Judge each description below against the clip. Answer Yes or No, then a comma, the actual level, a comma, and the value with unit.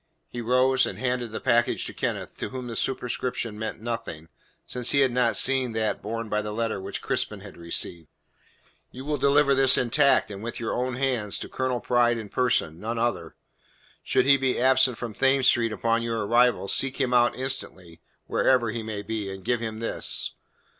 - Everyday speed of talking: Yes, average, 195 wpm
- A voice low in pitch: Yes, low, 120 Hz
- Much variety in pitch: No, average, 2.8 semitones